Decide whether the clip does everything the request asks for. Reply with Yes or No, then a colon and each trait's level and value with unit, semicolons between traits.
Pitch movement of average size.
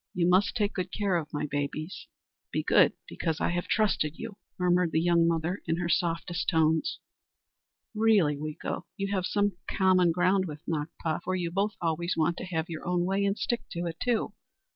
Yes: average, 3.0 semitones